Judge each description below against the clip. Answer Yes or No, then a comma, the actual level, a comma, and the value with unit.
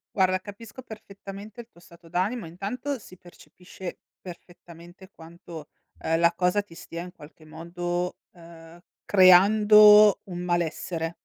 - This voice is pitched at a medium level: Yes, medium, 180 Hz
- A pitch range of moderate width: Yes, average, 3.1 semitones